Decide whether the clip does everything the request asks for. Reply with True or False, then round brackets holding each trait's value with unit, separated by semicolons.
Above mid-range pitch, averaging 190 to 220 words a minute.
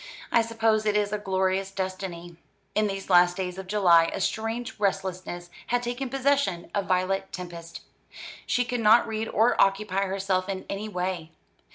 False (195 Hz; 165 wpm)